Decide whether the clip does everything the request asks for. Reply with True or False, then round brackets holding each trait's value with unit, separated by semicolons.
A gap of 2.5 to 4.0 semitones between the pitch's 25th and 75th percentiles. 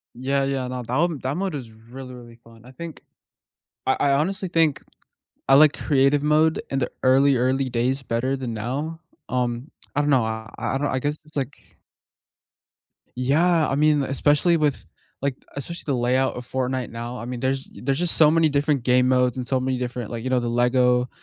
True (2.8 semitones)